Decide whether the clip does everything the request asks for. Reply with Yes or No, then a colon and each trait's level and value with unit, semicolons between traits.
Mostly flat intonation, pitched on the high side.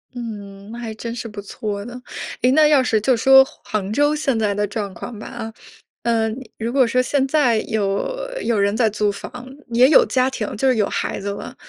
No: average, 3.5 semitones; high, 230 Hz